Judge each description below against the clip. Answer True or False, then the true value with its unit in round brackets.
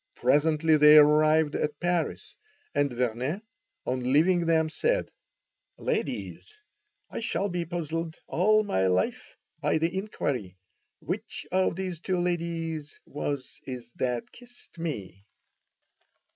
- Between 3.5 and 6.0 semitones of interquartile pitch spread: True (3.9 semitones)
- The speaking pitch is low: False (160 Hz)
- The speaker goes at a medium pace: False (115 wpm)